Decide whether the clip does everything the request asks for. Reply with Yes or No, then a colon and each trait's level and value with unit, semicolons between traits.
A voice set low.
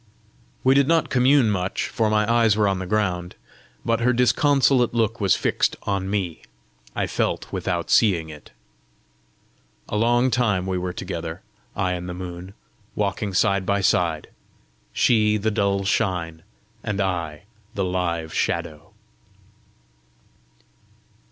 Yes: low, 100 Hz